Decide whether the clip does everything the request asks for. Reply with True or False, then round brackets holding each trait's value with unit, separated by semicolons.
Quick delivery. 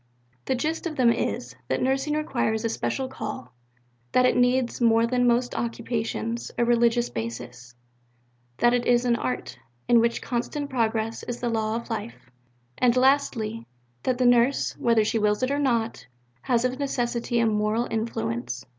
False (165 wpm)